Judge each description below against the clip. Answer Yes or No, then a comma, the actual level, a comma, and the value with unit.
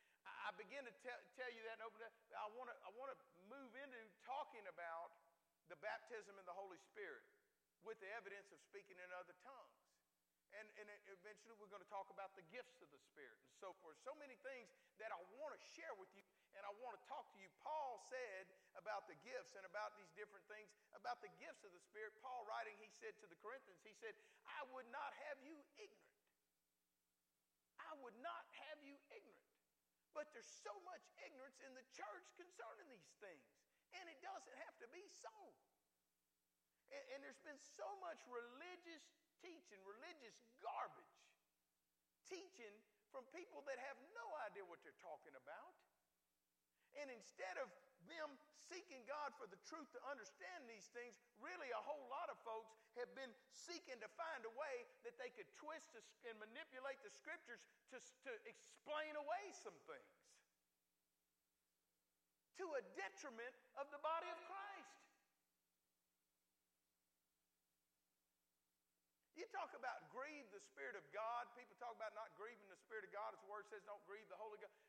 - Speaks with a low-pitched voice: No, high, 235 Hz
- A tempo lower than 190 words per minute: Yes, average, 170 wpm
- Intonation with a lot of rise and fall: Yes, wide, 8.6 semitones